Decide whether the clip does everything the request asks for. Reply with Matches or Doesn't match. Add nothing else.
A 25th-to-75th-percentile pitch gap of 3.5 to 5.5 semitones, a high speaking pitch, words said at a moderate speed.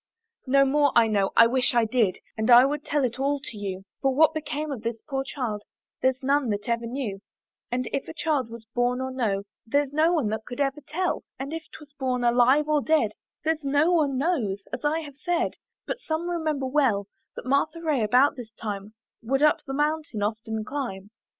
Doesn't match